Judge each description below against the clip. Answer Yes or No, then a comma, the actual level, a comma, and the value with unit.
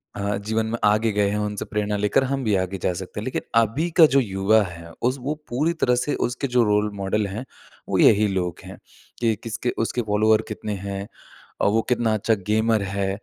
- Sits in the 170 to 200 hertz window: No, low, 105 Hz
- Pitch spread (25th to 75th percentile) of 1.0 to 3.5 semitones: Yes, average, 2.9 semitones